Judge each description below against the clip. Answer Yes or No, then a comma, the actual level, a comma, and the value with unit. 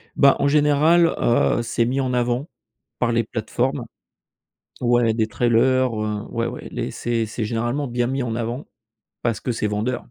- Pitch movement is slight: Yes, narrow, 2.2 semitones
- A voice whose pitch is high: No, low, 120 Hz